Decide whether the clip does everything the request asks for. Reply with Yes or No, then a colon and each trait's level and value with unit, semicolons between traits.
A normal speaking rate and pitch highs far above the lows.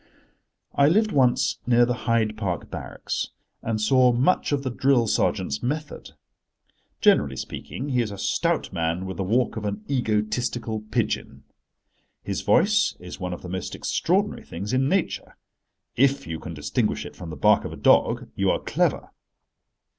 Yes: average, 165 wpm; wide, 6.0 semitones